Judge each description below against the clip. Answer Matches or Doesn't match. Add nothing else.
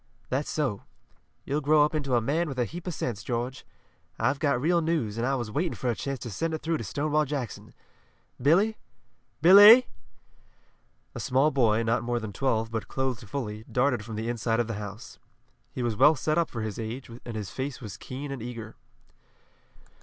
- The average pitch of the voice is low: Matches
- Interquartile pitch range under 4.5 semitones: Doesn't match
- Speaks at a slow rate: Doesn't match